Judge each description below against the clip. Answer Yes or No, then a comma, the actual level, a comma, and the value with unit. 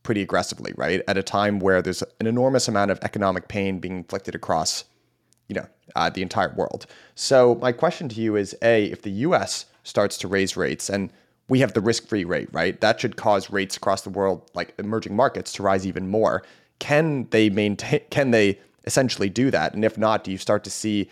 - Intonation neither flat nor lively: Yes, average, 3.0 semitones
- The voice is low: Yes, low, 105 Hz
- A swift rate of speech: Yes, fast, 210 wpm